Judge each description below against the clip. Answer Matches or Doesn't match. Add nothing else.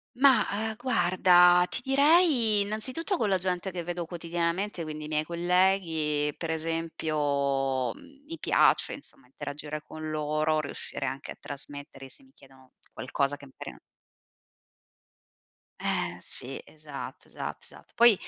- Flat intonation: Doesn't match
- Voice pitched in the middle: Matches